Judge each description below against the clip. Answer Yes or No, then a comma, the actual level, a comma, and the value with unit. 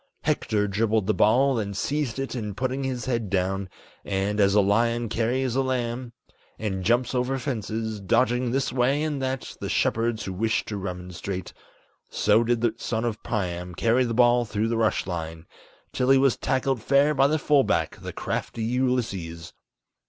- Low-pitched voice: Yes, low, 115 Hz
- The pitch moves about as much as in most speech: Yes, average, 4.0 semitones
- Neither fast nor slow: Yes, average, 175 wpm